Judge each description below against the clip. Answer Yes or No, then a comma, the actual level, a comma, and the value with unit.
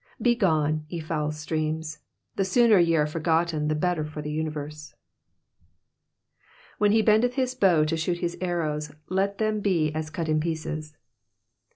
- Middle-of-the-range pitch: Yes, medium, 160 Hz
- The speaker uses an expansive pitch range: No, average, 3.5 semitones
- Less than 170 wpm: Yes, average, 155 wpm